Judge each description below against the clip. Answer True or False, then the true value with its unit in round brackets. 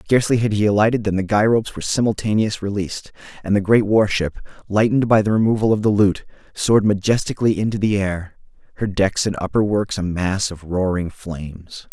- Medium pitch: False (100 Hz)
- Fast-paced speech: False (185 wpm)